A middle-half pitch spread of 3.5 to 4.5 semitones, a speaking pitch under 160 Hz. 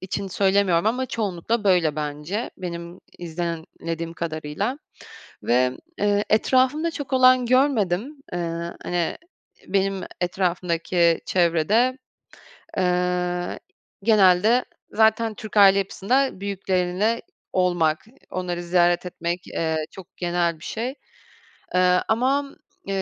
No: average, 4.2 semitones; medium, 185 Hz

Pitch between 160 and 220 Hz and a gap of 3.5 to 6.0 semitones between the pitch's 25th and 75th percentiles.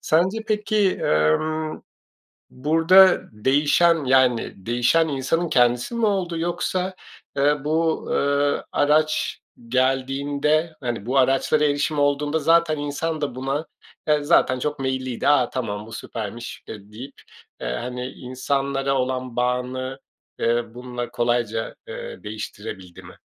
No: low, 135 Hz; average, 4.1 semitones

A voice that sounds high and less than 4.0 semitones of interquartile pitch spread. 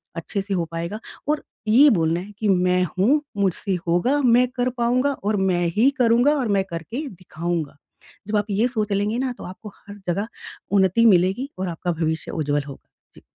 No: high, 200 Hz; average, 5.2 semitones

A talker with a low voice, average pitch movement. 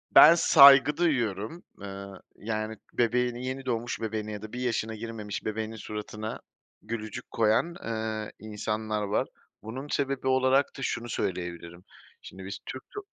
Yes: low, 110 Hz; average, 3.4 semitones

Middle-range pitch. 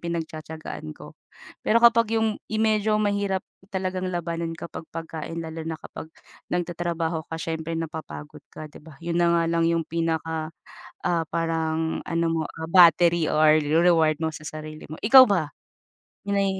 Yes: medium, 165 Hz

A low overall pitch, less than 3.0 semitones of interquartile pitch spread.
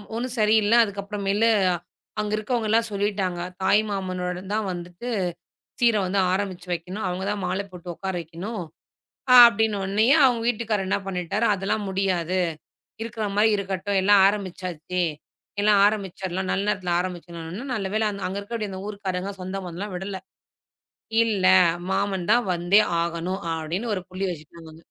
No: high, 195 Hz; narrow, 2.6 semitones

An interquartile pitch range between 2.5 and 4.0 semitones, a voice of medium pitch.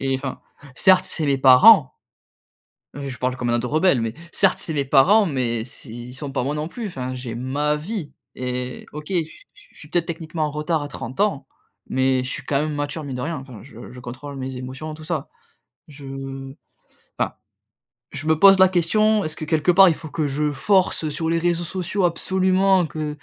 No: average, 4.7 semitones; medium, 150 Hz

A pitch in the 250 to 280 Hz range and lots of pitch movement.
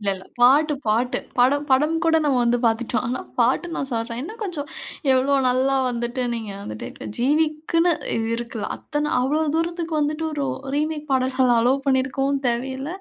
No: very high, 270 Hz; average, 3.9 semitones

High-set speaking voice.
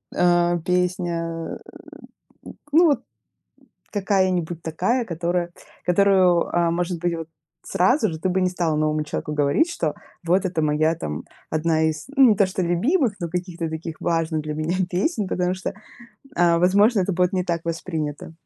No: medium, 175 Hz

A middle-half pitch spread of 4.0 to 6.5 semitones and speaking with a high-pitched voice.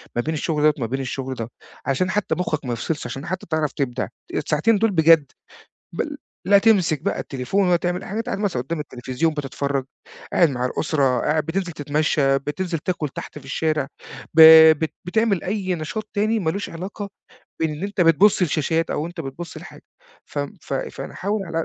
No: average, 4.7 semitones; medium, 160 Hz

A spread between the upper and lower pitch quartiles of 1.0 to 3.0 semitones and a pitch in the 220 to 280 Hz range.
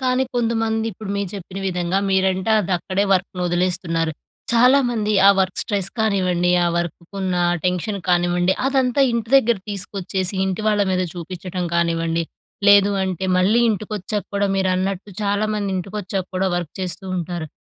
No: average, 2.7 semitones; high, 190 Hz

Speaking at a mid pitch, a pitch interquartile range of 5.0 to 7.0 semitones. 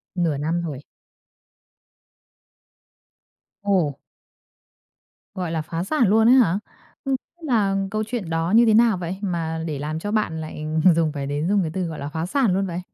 No: medium, 175 Hz; average, 4.5 semitones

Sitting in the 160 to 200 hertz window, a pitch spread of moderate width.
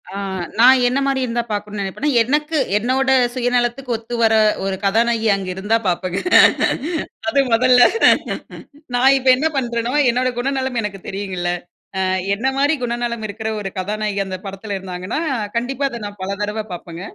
No: high, 230 Hz; average, 4.0 semitones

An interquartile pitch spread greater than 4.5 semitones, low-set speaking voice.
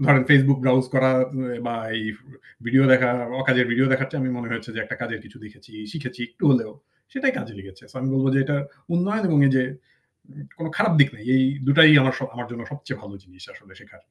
No: average, 2.9 semitones; low, 130 Hz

